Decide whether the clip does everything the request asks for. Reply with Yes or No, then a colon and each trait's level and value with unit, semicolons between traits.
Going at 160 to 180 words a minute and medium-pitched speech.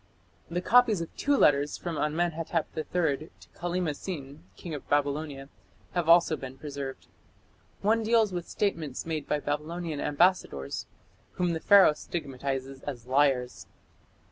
No: slow, 135 wpm; medium, 155 Hz